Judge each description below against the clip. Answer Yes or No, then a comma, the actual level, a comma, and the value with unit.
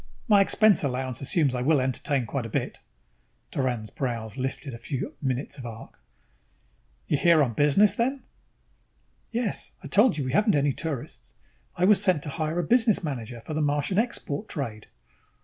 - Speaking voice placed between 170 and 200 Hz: No, medium, 145 Hz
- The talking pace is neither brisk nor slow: Yes, average, 170 wpm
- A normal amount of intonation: No, wide, 6.3 semitones